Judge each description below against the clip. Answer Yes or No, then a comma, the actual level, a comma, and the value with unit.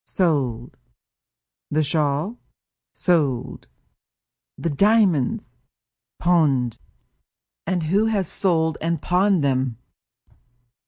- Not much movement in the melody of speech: No, average, 5.0 semitones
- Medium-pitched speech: Yes, medium, 160 Hz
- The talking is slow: Yes, slow, 75 wpm